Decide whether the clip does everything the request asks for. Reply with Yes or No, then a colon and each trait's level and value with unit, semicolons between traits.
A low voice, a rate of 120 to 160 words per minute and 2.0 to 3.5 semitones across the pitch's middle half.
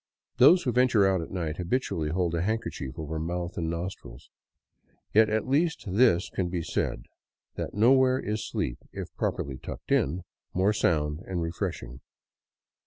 No: very low, 90 Hz; average, 155 wpm; average, 5.3 semitones